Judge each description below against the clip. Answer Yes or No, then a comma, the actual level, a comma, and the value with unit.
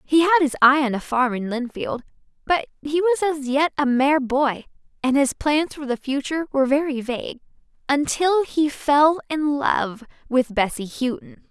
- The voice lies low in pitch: No, very high, 280 Hz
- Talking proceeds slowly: No, average, 175 wpm